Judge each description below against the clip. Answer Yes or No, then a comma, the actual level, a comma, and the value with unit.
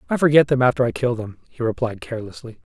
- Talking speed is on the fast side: Yes, fast, 220 wpm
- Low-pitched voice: Yes, low, 120 Hz